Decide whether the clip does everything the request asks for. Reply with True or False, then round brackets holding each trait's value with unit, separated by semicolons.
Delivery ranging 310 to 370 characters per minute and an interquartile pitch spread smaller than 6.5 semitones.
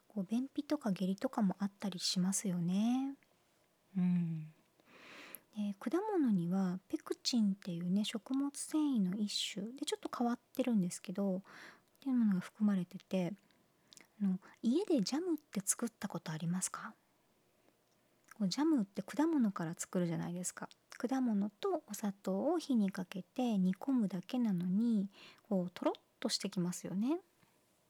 False (270 characters per minute; 5.7 semitones)